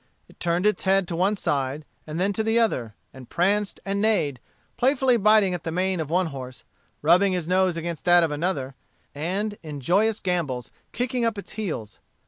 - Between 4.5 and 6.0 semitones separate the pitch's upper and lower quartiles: Yes, average, 4.9 semitones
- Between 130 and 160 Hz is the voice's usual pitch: No, medium, 180 Hz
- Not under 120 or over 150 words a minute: No, average, 190 wpm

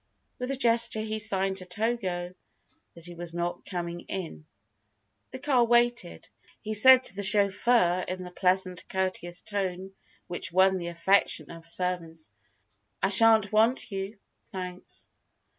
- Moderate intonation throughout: Yes, average, 3.6 semitones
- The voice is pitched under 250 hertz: Yes, high, 190 Hz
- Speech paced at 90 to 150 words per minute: Yes, average, 145 wpm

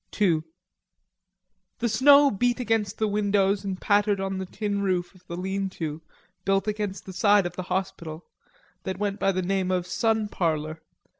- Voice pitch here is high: Yes, high, 195 Hz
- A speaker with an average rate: Yes, average, 170 wpm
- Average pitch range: No, narrow, 2.3 semitones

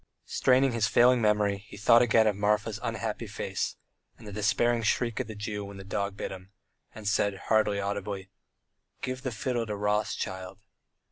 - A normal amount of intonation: No, narrow, 2.3 semitones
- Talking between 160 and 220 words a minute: Yes, average, 175 wpm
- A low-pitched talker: Yes, low, 105 Hz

